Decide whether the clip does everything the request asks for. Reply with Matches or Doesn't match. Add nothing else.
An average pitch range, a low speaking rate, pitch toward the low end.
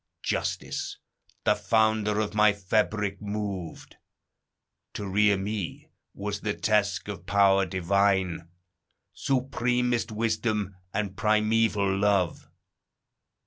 Doesn't match